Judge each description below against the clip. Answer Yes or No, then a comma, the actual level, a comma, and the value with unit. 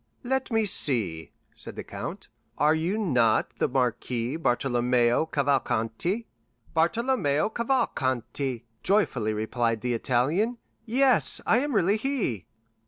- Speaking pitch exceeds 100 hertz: Yes, medium, 140 Hz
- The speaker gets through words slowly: Yes, slow, 110 wpm